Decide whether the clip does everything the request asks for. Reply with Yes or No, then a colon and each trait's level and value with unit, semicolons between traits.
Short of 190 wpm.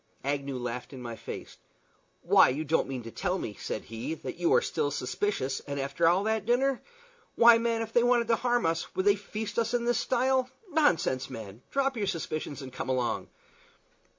No: average, 195 wpm